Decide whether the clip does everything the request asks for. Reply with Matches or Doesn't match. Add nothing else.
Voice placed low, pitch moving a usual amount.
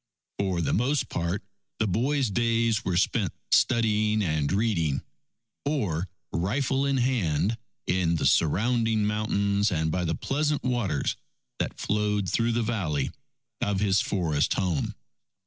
Matches